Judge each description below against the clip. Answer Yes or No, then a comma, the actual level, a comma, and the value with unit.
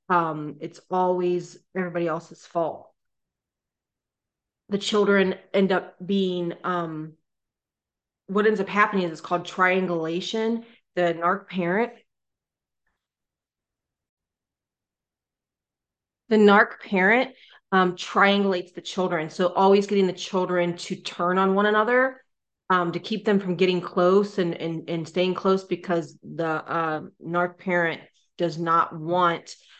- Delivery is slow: Yes, slow, 120 wpm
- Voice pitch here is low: No, medium, 180 Hz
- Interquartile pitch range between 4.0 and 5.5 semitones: No, narrow, 2.4 semitones